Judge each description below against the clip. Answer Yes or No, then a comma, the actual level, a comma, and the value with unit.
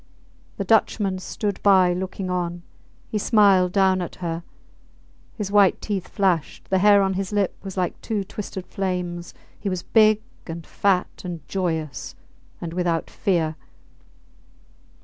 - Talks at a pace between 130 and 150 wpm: Yes, average, 140 wpm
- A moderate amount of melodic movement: No, narrow, 2.2 semitones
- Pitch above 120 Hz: Yes, medium, 185 Hz